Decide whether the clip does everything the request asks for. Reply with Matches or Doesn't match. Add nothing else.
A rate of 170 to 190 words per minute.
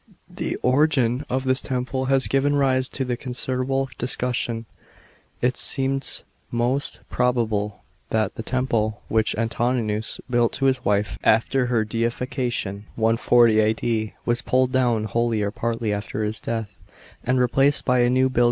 Doesn't match